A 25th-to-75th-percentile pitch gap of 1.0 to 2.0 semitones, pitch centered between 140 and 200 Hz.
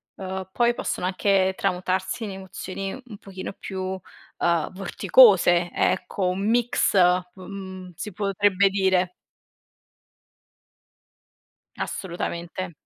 Yes: narrow, 1.3 semitones; high, 190 Hz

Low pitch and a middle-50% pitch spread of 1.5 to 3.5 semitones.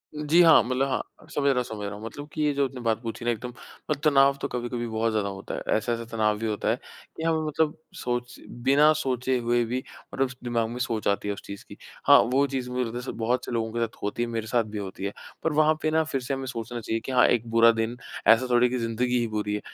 Yes: low, 120 Hz; average, 2.9 semitones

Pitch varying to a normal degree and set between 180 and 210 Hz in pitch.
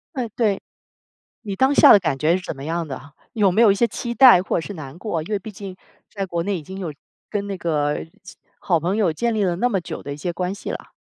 Yes: average, 4.0 semitones; medium, 185 Hz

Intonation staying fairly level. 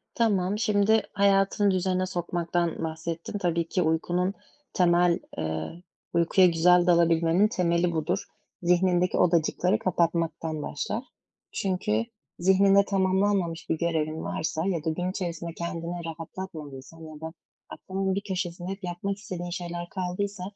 Yes: narrow, 2.3 semitones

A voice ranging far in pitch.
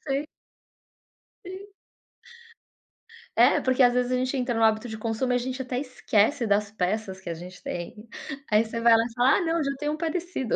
No: average, 3.8 semitones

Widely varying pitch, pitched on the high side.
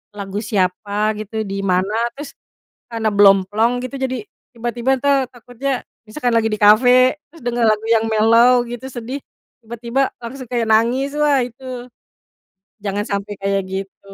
No: average, 3.2 semitones; high, 230 Hz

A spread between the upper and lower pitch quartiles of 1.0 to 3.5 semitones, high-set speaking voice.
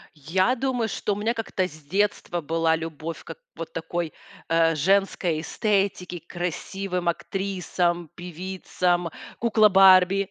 No: average, 2.9 semitones; medium, 180 Hz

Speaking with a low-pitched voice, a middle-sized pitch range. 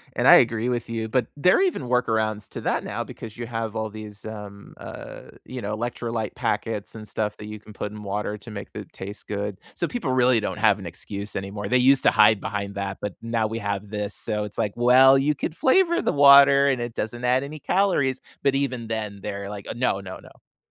Yes: low, 110 Hz; average, 3.5 semitones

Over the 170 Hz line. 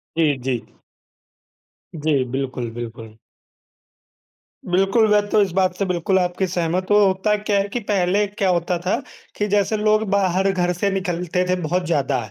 Yes: medium, 185 Hz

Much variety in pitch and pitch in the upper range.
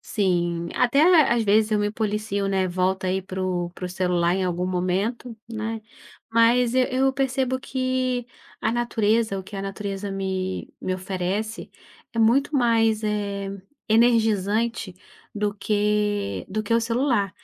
No: average, 3.4 semitones; high, 210 Hz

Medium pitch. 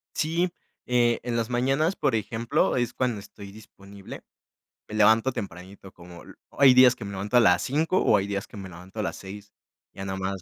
No: low, 105 Hz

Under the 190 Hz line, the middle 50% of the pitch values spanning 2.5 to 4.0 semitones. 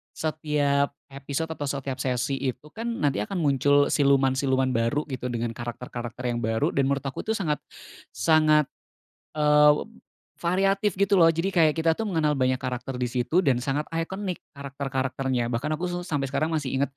Yes: medium, 140 Hz; average, 3.7 semitones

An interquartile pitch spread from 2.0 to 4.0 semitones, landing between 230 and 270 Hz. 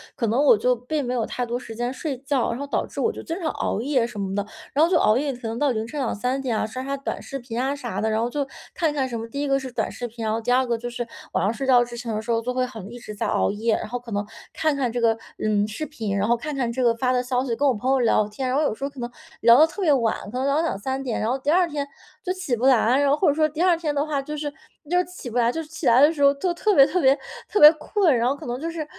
Yes: average, 3.7 semitones; very high, 255 Hz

